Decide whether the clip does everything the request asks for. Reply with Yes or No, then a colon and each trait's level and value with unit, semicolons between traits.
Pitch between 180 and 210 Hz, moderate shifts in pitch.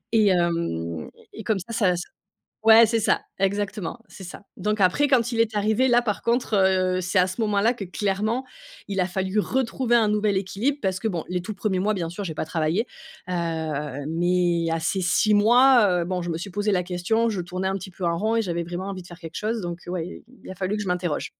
Yes: high, 190 Hz; average, 3.6 semitones